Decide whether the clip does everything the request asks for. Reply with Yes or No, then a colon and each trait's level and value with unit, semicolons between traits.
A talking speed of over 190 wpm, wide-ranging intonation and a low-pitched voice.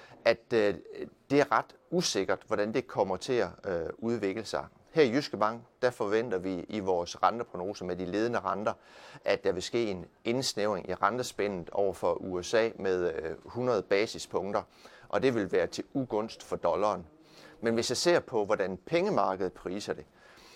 No: average, 165 wpm; wide, 6.1 semitones; low, 115 Hz